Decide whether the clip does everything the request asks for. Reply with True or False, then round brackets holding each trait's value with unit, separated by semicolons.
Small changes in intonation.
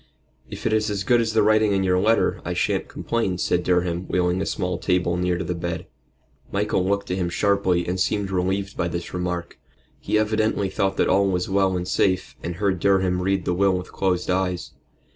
True (1.9 semitones)